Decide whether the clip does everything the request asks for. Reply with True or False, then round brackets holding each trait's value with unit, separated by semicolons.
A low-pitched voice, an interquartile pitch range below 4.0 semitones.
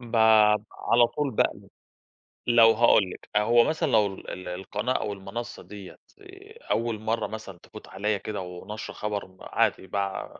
True (105 Hz; 3.0 semitones)